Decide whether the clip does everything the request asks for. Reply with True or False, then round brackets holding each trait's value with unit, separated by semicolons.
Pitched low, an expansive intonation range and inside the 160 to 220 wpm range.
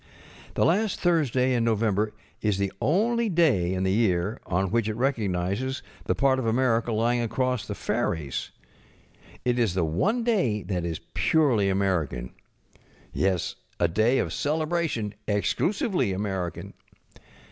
False (115 Hz; 6.0 semitones; 135 wpm)